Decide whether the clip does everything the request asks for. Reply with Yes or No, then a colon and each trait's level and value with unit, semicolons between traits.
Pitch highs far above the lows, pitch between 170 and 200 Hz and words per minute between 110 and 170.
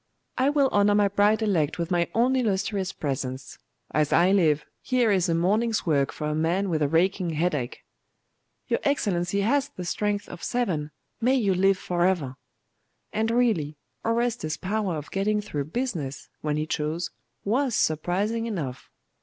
Yes: wide, 5.7 semitones; medium, 185 Hz; average, 160 wpm